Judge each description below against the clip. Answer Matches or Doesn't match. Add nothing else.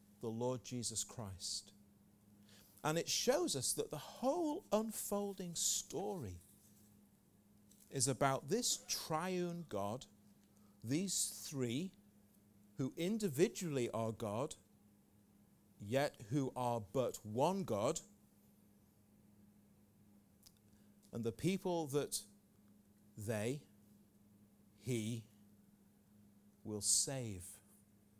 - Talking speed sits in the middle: Doesn't match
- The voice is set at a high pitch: Doesn't match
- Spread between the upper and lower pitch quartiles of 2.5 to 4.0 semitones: Doesn't match